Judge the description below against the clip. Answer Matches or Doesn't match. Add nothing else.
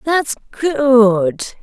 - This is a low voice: Doesn't match